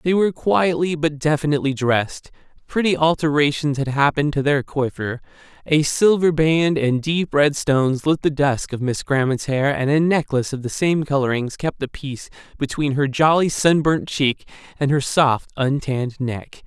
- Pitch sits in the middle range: Yes, medium, 145 Hz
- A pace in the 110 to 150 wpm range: No, average, 175 wpm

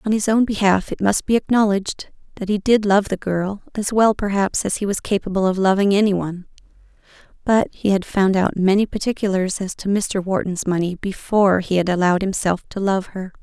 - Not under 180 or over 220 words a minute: Yes, average, 195 wpm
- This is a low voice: No, high, 195 Hz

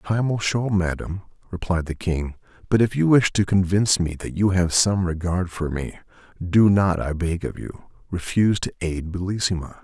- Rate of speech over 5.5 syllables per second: No, 4.9 syllables/s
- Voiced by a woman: No, male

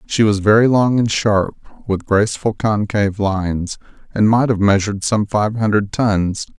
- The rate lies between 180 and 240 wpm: No, average, 165 wpm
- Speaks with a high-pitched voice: No, low, 105 Hz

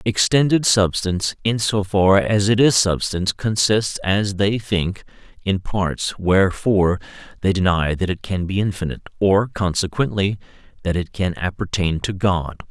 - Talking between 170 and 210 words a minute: No, average, 145 wpm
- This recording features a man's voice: Yes, male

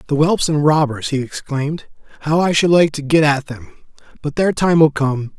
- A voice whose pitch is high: No, medium, 150 Hz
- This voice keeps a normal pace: No, fast, 210 wpm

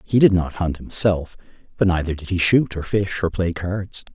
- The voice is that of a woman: No, male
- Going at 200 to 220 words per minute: Yes, fast, 205 wpm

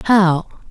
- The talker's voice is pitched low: No, medium, 185 Hz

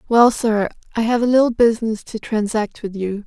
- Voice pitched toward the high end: Yes, high, 225 Hz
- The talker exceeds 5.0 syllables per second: Yes, 5.3 syllables/s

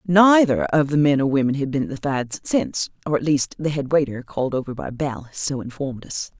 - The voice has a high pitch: No, medium, 140 Hz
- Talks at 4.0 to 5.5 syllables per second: No, 5.7 syllables/s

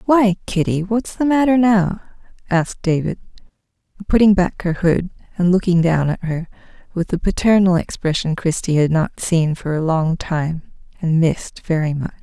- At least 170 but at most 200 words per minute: No, average, 160 wpm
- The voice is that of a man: No, female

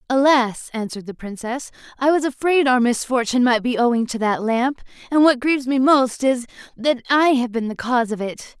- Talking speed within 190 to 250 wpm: Yes, average, 200 wpm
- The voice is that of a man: No, female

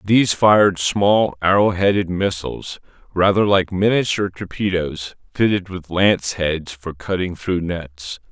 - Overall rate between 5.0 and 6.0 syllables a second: No, 4.4 syllables/s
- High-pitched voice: No, very low, 90 Hz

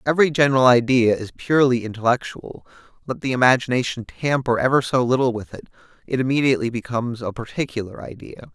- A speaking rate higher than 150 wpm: No, average, 145 wpm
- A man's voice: Yes, male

